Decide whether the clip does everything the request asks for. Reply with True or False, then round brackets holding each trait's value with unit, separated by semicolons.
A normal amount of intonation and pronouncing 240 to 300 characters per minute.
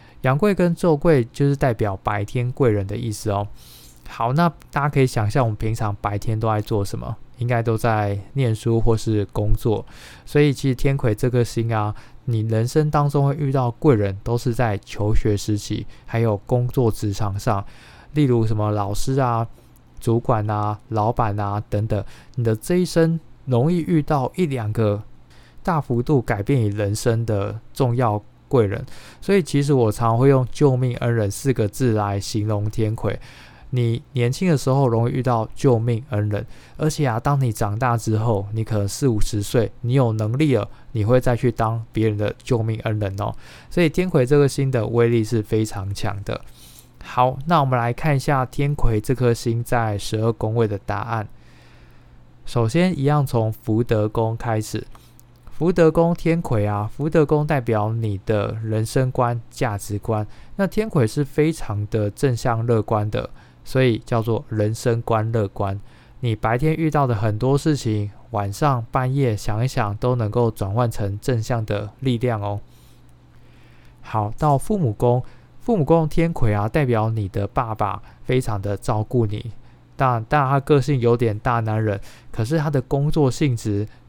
True (3.8 semitones; 245 characters per minute)